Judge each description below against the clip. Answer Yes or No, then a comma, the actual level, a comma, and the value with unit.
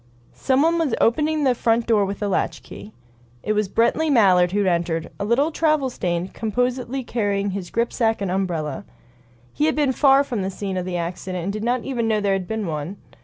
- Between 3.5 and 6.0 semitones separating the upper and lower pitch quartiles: Yes, average, 5.1 semitones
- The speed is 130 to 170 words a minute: No, fast, 205 wpm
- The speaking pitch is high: Yes, high, 215 Hz